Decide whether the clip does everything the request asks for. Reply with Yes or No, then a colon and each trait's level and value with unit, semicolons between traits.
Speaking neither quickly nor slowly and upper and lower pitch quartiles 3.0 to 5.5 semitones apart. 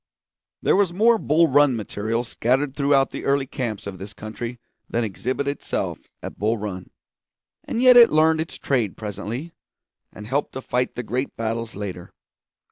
Yes: average, 165 wpm; average, 5.0 semitones